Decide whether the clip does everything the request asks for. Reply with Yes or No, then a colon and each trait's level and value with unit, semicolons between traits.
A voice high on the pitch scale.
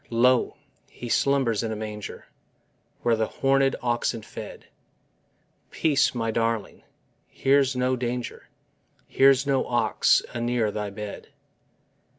No: low, 120 Hz